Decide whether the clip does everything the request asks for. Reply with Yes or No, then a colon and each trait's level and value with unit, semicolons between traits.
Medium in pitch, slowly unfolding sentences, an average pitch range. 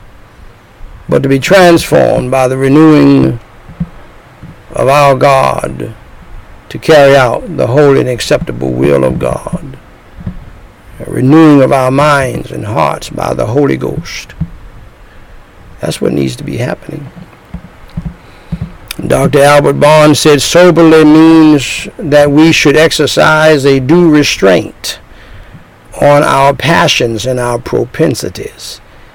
Yes: medium, 145 Hz; slow, 115 wpm; average, 3.1 semitones